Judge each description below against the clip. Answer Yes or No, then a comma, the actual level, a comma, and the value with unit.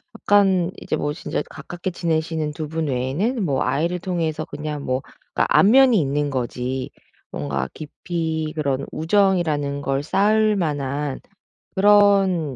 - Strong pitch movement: No, average, 4.8 semitones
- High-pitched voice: No, medium, 155 Hz